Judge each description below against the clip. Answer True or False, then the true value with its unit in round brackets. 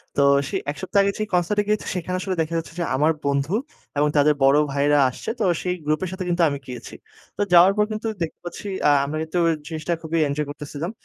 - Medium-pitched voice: True (160 Hz)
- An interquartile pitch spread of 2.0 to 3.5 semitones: False (3.9 semitones)